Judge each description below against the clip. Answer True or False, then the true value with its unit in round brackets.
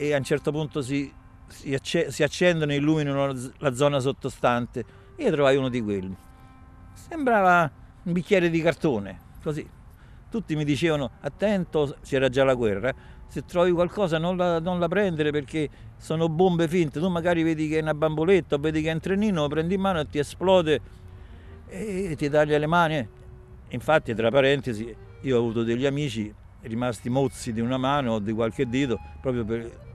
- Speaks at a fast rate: True (175 wpm)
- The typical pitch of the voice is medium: True (145 Hz)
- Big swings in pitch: True (5.9 semitones)